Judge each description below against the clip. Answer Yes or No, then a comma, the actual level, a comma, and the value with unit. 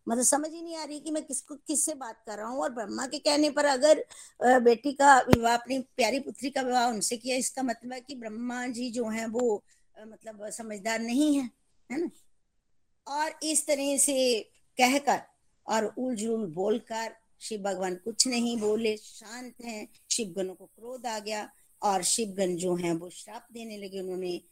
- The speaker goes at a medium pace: Yes, average, 170 wpm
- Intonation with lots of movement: No, average, 3.9 semitones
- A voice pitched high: Yes, high, 235 Hz